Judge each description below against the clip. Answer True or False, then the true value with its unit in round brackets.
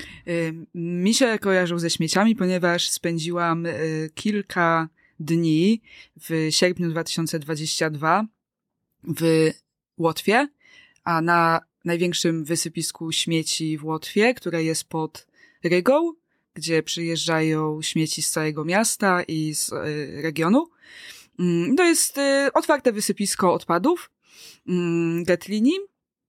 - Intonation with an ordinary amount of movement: True (4.2 semitones)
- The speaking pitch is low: False (170 Hz)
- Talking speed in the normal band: False (90 wpm)